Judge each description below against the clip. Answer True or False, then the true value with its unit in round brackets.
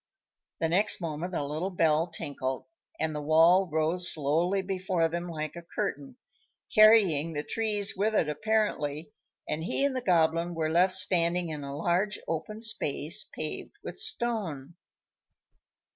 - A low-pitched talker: False (170 Hz)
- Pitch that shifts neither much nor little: True (4.0 semitones)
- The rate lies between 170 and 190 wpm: False (145 wpm)